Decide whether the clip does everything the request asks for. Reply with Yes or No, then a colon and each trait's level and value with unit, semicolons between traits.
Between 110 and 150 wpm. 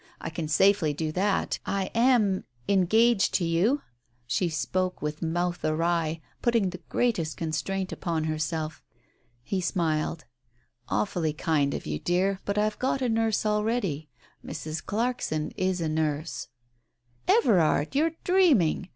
Yes: average, 140 wpm